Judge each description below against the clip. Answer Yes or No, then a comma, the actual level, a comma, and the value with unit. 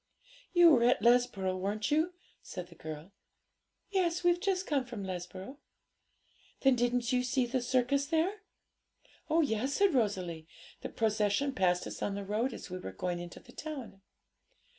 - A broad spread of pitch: Yes, wide, 6.8 semitones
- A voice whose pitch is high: Yes, high, 245 Hz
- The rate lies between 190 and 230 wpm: No, average, 160 wpm